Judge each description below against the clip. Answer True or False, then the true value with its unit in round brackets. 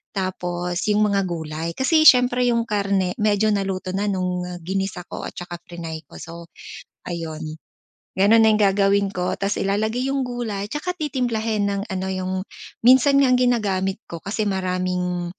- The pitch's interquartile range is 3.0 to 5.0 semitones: True (3.6 semitones)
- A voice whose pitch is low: False (195 Hz)